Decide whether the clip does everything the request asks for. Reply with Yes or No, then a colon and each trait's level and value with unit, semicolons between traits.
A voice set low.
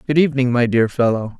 Yes: low, 125 Hz